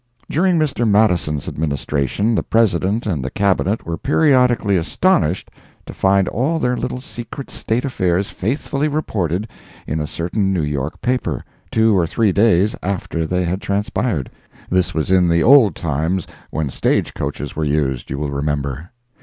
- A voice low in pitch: Yes, very low, 95 Hz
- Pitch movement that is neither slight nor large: No, wide, 6.4 semitones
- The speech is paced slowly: No, average, 155 wpm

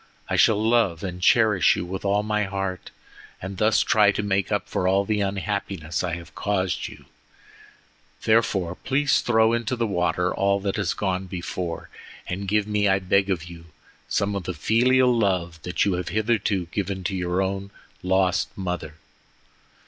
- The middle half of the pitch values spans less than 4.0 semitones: Yes, narrow, 2.6 semitones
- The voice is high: No, very low, 95 Hz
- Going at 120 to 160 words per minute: No, average, 170 wpm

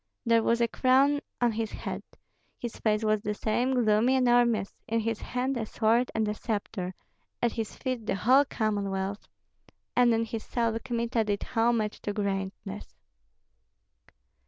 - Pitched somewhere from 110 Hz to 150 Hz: No, high, 225 Hz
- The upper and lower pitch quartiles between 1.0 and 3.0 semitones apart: Yes, narrow, 2.4 semitones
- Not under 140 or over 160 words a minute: Yes, average, 155 wpm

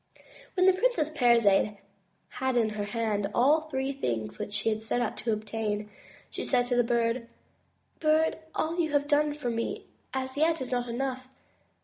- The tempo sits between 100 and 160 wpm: No, average, 185 wpm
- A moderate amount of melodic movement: Yes, average, 4.9 semitones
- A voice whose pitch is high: Yes, high, 245 Hz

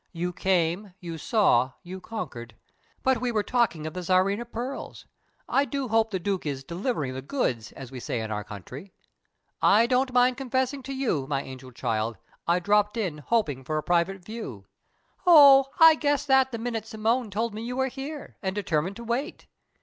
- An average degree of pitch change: No, wide, 8.2 semitones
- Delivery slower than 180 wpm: No, average, 190 wpm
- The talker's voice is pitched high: Yes, high, 205 Hz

